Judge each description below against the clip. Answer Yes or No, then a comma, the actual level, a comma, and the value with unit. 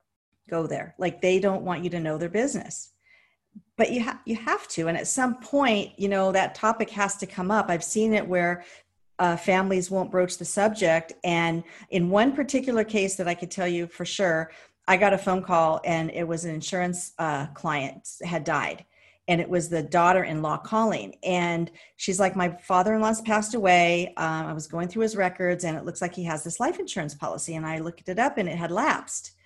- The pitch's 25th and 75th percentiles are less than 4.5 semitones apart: Yes, average, 3.5 semitones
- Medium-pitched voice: Yes, medium, 180 Hz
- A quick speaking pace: Yes, fast, 210 wpm